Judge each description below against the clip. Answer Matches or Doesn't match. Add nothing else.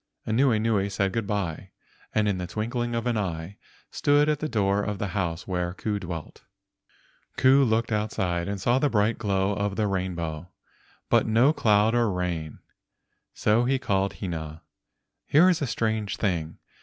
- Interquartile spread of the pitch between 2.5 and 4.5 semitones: Matches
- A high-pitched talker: Doesn't match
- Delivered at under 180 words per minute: Matches